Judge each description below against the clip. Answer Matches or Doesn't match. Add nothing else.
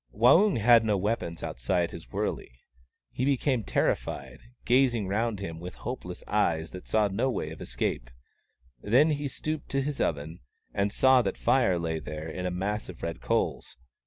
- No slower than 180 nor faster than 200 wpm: Doesn't match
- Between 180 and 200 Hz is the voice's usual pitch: Doesn't match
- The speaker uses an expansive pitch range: Matches